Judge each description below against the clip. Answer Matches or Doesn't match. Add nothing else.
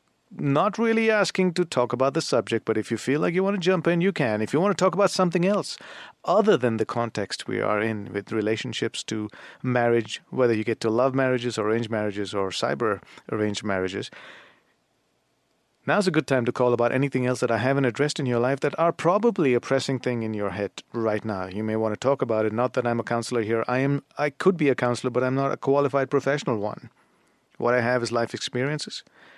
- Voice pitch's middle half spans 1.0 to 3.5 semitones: Doesn't match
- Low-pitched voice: Matches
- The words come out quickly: Matches